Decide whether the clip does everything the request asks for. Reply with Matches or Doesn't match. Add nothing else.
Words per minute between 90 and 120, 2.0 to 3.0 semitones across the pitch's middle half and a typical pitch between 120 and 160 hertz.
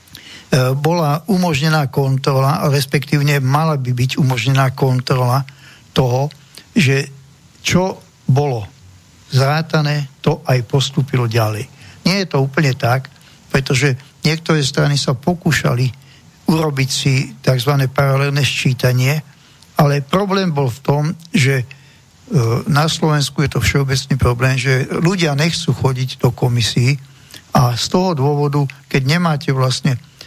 Matches